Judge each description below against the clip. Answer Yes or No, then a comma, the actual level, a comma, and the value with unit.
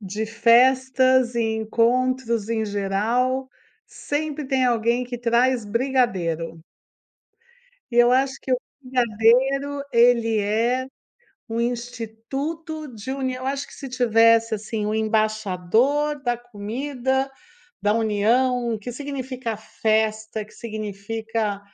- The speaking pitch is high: Yes, high, 235 Hz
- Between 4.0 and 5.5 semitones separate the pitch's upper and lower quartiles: No, average, 3.0 semitones